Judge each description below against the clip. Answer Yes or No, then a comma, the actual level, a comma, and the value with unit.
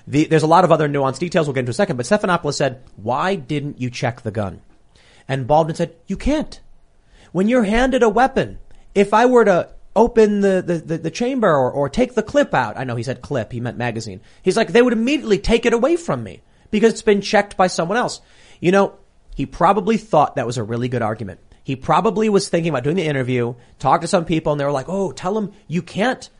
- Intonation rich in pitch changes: Yes, wide, 8.0 semitones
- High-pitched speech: No, medium, 170 Hz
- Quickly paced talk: Yes, fast, 240 wpm